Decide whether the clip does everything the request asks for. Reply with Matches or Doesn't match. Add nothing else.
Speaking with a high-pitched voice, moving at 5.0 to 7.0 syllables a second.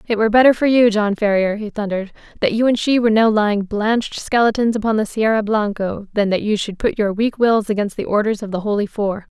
Matches